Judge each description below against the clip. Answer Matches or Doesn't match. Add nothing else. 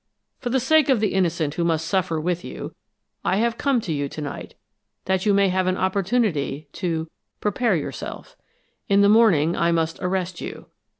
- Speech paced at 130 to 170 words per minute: Doesn't match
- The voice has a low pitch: Doesn't match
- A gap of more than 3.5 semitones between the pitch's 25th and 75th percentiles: Matches